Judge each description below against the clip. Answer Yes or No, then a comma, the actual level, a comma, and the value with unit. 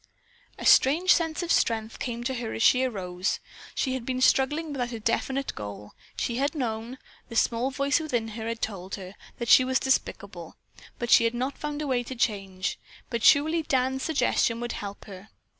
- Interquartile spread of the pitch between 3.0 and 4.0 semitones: Yes, average, 3.3 semitones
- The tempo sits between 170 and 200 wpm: Yes, average, 190 wpm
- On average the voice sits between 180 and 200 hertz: No, high, 245 Hz